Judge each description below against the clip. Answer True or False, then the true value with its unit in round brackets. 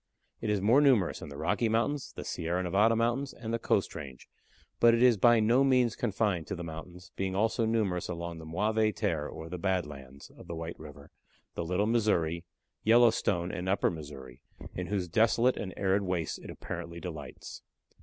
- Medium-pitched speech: False (95 Hz)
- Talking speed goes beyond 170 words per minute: True (190 wpm)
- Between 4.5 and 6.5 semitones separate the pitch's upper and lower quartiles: True (5.2 semitones)